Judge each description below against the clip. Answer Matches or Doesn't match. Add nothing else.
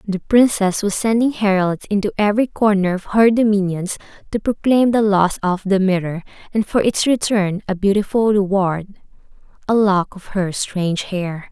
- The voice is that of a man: Doesn't match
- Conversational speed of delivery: Matches